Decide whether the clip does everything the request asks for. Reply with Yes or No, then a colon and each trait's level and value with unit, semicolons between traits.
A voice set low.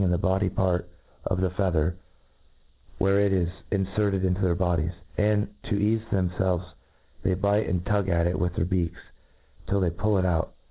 Yes: very low, 95 Hz